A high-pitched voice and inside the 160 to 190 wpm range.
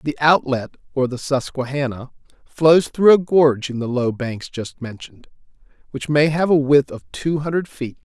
No: low, 135 Hz; average, 175 wpm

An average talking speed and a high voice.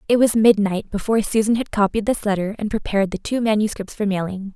No: fast, 210 wpm; high, 210 Hz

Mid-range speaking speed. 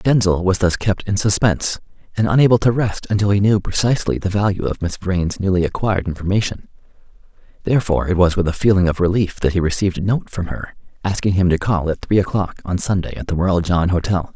No: fast, 215 wpm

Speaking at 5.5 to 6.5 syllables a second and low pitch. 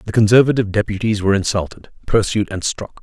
Yes: 6.3 syllables/s; low, 105 Hz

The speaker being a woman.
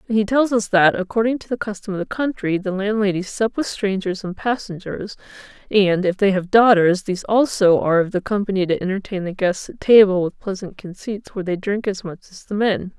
Yes: female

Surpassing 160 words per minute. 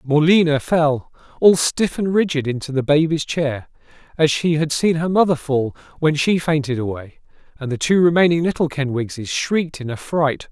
Yes: average, 170 wpm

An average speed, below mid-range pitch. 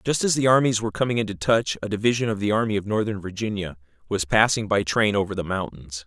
No: fast, 230 wpm; low, 105 Hz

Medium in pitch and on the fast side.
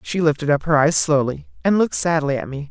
Yes: medium, 155 Hz; fast, 245 wpm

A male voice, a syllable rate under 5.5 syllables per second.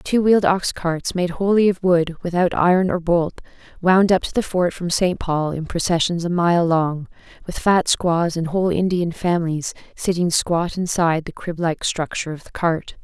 No: female; 4.8 syllables/s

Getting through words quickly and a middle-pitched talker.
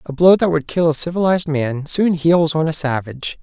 Yes: fast, 230 wpm; medium, 160 Hz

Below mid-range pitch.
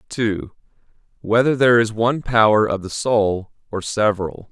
Yes: low, 110 Hz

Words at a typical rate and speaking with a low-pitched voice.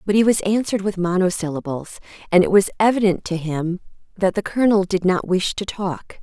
No: average, 195 wpm; medium, 185 Hz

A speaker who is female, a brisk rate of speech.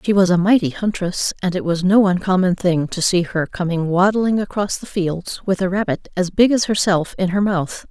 Yes: female; fast, 220 wpm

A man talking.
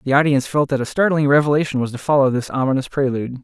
Yes: male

